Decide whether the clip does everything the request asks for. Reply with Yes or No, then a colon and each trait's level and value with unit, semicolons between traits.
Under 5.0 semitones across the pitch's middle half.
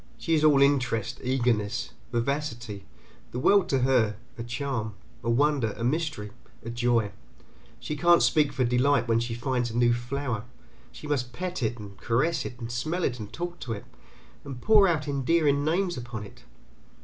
Yes: average, 4.2 semitones